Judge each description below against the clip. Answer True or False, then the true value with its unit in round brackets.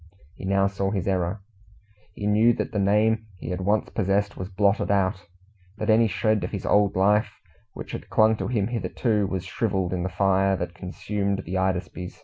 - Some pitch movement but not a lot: False (2.0 semitones)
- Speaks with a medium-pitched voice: False (100 Hz)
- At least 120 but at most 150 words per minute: False (190 wpm)